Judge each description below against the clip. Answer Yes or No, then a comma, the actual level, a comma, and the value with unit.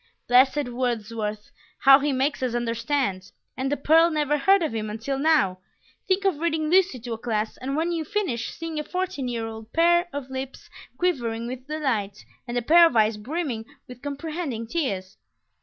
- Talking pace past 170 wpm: Yes, average, 180 wpm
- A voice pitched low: No, very high, 270 Hz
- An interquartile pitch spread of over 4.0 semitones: Yes, wide, 5.6 semitones